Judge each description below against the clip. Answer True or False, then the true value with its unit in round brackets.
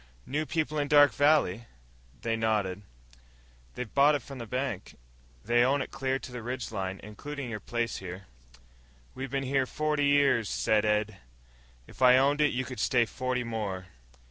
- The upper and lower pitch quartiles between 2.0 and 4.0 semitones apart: False (4.4 semitones)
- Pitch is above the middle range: False (125 Hz)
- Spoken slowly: False (170 wpm)